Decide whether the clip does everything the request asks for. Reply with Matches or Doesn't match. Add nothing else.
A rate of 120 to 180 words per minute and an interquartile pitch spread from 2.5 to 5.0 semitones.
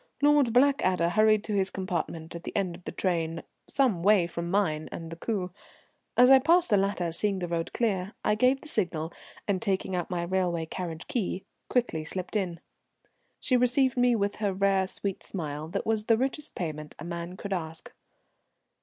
Doesn't match